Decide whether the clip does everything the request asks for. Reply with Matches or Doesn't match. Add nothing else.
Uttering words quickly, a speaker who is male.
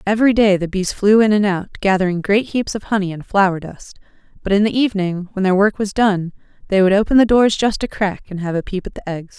Doesn't match